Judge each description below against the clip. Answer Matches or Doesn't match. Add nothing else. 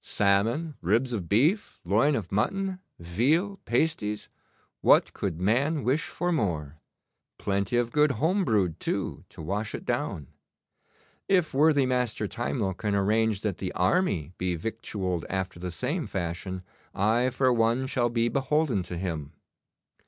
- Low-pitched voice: Matches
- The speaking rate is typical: Matches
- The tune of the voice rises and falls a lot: Matches